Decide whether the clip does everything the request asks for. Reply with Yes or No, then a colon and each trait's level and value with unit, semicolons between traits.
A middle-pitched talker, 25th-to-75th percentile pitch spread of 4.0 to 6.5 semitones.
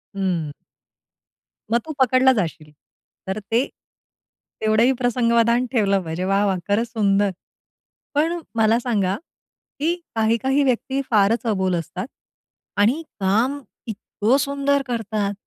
No: high, 225 Hz; average, 4.4 semitones